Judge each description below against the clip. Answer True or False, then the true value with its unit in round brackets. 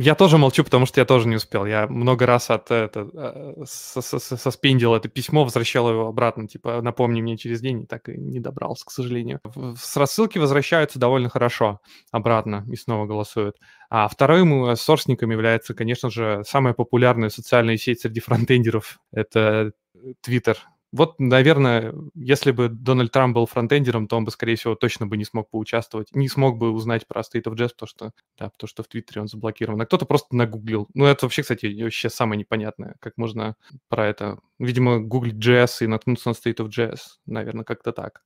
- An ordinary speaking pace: False (185 wpm)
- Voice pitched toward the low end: True (120 Hz)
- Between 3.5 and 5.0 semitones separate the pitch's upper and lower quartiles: False (2.5 semitones)